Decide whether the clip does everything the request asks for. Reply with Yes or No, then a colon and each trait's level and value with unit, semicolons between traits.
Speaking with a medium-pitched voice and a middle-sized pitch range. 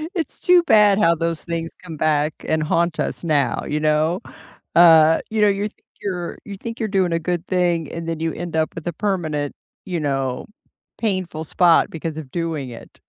Yes: medium, 165 Hz; average, 3.0 semitones